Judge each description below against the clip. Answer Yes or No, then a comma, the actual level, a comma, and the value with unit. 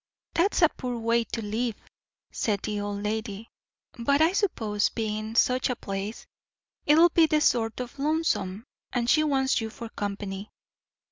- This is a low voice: No, high, 230 Hz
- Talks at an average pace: Yes, average, 150 wpm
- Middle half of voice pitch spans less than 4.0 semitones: No, average, 4.6 semitones